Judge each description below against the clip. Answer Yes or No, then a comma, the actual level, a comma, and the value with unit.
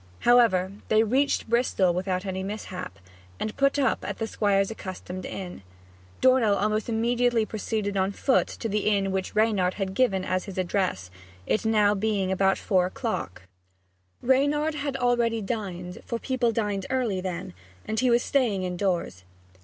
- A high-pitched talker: Yes, high, 210 Hz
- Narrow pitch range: No, average, 4.0 semitones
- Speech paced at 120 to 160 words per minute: Yes, average, 155 wpm